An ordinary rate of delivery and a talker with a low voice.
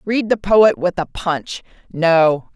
No: average, 165 wpm; medium, 180 Hz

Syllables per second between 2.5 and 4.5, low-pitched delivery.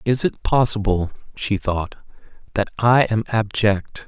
Yes: 4.0 syllables/s; low, 105 Hz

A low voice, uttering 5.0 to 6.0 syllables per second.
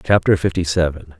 Yes: very low, 85 Hz; 5.6 syllables/s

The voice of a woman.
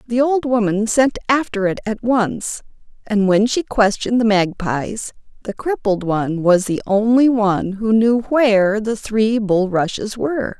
Yes: female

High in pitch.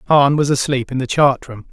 No: low, 135 Hz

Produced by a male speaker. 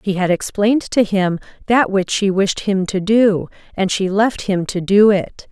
No: female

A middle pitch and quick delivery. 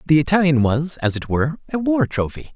Yes: medium, 155 Hz; fast, 210 wpm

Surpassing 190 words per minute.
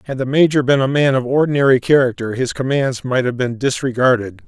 Yes: average, 200 wpm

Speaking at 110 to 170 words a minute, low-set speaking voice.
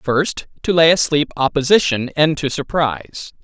No: average, 140 wpm; medium, 150 Hz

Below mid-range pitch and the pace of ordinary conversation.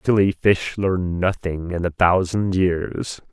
Yes: very low, 90 Hz; average, 145 wpm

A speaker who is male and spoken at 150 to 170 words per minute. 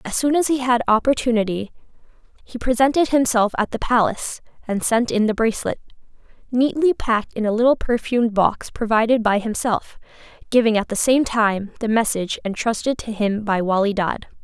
No: female; average, 165 wpm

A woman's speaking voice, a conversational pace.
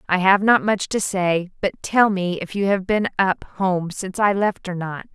No: female; fast, 235 wpm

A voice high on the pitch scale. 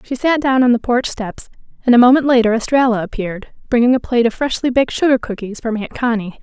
Yes: high, 240 Hz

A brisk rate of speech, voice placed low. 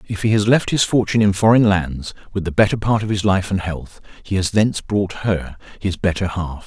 Yes: fast, 235 wpm; low, 100 Hz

